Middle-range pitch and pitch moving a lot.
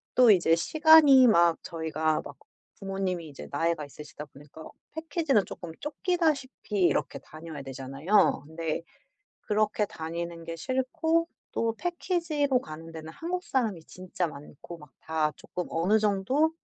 Yes: medium, 180 Hz; wide, 8.5 semitones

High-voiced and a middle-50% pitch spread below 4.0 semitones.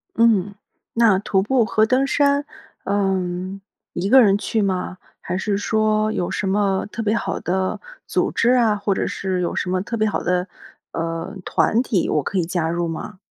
Yes: high, 200 Hz; average, 3.0 semitones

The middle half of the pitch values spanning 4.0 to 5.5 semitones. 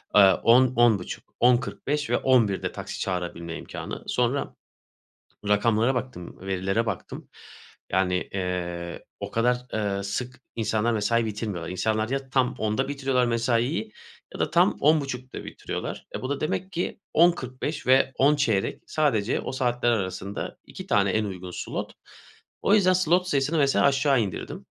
Yes: average, 5.1 semitones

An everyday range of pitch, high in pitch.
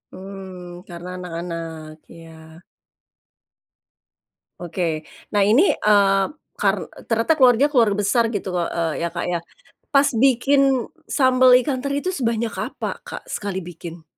No: wide, 6.5 semitones; high, 200 Hz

